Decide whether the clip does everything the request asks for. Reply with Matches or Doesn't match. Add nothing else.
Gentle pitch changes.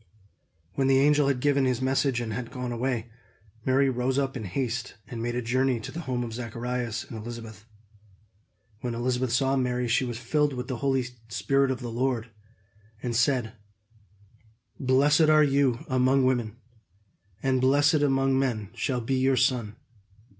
Matches